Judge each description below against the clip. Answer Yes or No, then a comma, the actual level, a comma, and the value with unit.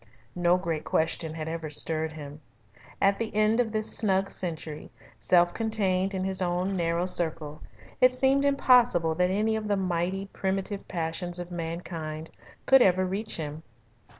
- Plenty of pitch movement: No, average, 3.7 semitones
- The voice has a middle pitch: Yes, medium, 180 Hz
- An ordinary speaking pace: Yes, average, 155 wpm